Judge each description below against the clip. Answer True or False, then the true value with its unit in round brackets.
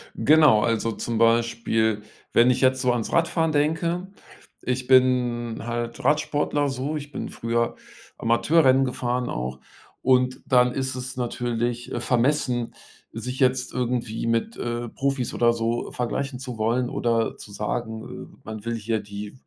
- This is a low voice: True (120 Hz)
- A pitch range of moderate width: False (2.1 semitones)